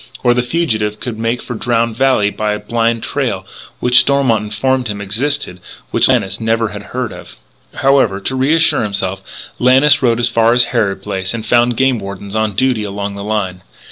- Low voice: Yes, low, 115 Hz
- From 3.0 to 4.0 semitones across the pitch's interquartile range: Yes, average, 3.3 semitones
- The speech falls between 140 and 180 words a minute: No, average, 190 wpm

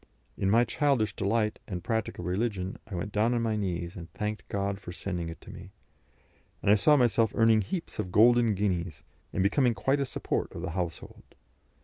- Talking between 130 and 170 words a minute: No, average, 195 wpm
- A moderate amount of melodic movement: Yes, average, 3.8 semitones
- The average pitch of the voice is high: No, low, 105 Hz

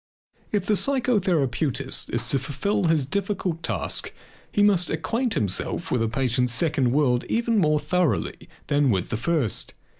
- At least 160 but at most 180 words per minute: No, average, 150 wpm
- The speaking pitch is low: No, medium, 155 Hz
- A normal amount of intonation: No, wide, 7.7 semitones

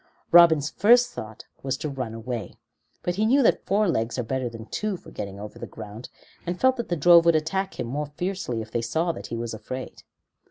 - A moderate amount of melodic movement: No, wide, 7.5 semitones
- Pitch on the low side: No, medium, 145 Hz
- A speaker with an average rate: No, fast, 225 wpm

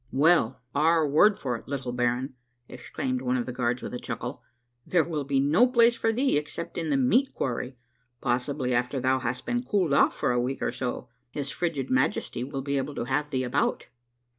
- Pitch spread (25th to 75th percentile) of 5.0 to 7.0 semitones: No, average, 3.7 semitones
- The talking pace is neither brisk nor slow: No, fast, 215 wpm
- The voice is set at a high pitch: No, low, 135 Hz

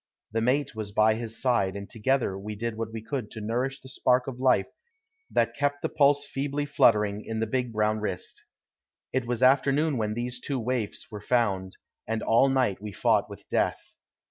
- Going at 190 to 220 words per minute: Yes, average, 195 wpm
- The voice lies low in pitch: Yes, low, 115 Hz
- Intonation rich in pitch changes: No, average, 3.7 semitones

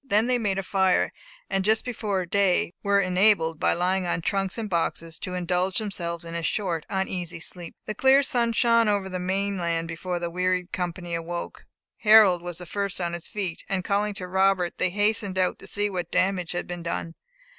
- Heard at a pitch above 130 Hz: Yes, medium, 185 Hz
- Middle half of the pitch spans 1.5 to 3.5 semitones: Yes, narrow, 2.6 semitones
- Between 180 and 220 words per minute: Yes, average, 200 wpm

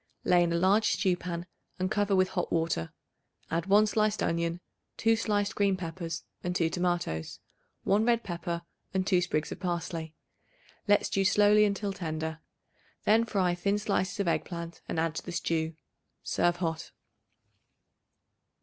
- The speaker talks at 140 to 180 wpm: Yes, average, 160 wpm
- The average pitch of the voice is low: No, medium, 180 Hz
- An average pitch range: Yes, average, 3.2 semitones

